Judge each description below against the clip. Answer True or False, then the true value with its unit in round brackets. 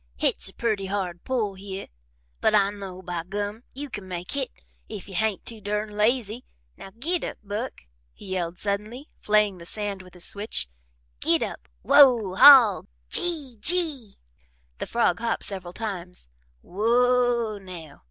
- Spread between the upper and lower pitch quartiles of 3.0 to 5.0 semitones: True (3.9 semitones)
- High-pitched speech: True (210 Hz)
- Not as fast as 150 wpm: False (155 wpm)